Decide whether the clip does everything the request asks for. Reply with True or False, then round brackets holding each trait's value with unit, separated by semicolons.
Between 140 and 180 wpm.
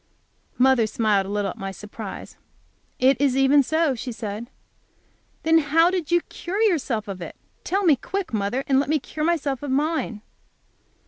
True (175 wpm)